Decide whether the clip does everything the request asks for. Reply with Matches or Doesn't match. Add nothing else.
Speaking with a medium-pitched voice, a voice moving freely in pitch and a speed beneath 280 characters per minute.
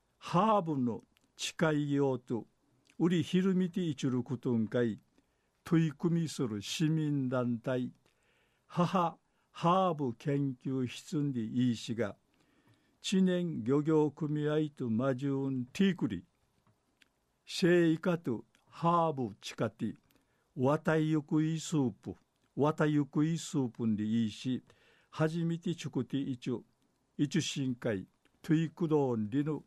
Doesn't match